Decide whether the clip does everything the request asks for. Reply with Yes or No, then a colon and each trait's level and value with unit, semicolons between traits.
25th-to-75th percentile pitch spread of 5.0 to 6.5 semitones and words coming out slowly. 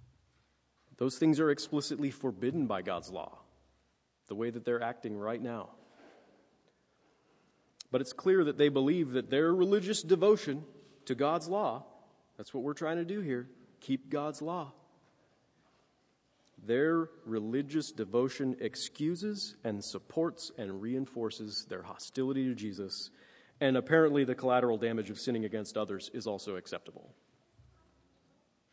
Yes: average, 5.3 semitones; slow, 130 wpm